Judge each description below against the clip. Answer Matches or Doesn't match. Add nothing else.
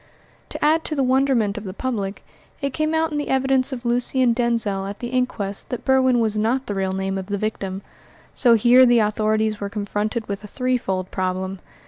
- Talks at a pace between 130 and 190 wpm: Doesn't match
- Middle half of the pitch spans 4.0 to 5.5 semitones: Matches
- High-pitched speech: Matches